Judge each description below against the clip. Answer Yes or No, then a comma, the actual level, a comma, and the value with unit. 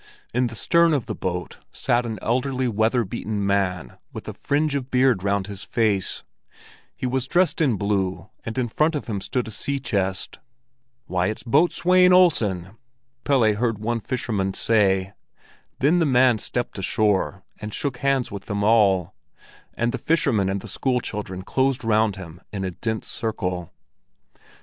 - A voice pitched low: Yes, low, 110 Hz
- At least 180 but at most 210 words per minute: No, average, 165 wpm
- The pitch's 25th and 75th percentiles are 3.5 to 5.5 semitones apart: Yes, average, 4.7 semitones